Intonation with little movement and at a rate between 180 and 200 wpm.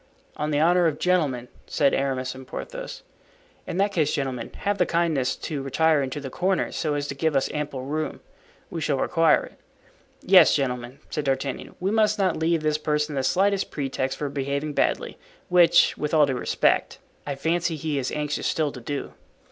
No: average, 3.5 semitones; average, 190 wpm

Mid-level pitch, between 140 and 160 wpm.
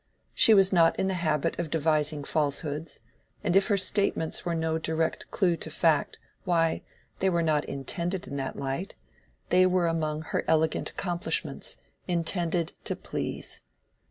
Yes: medium, 165 Hz; average, 150 wpm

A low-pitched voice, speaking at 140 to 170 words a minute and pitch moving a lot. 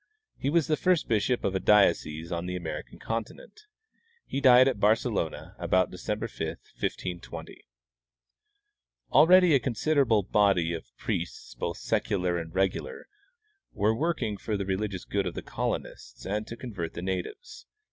Yes: low, 105 Hz; average, 150 wpm; wide, 5.8 semitones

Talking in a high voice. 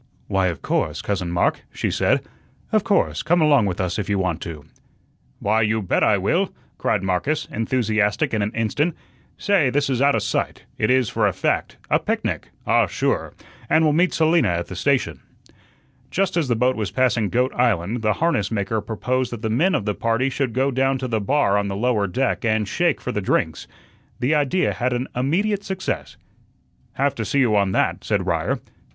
No: low, 120 Hz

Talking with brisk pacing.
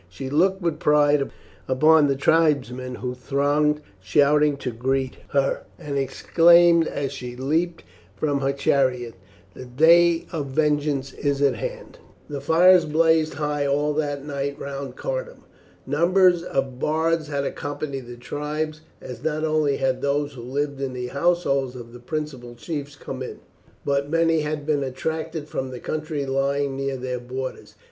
No: average, 155 wpm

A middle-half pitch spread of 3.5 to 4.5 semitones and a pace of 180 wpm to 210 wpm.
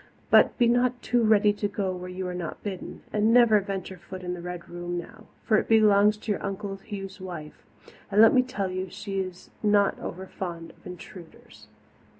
No: average, 2.8 semitones; average, 200 wpm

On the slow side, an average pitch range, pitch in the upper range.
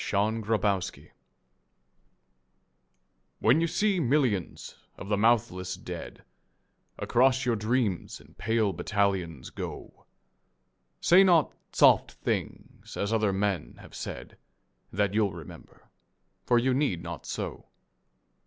No: slow, 120 wpm; average, 4.5 semitones; low, 105 Hz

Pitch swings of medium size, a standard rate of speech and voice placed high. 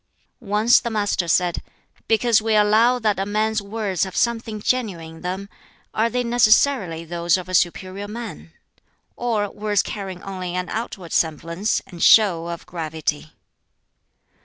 Yes: average, 3.9 semitones; average, 145 wpm; high, 200 Hz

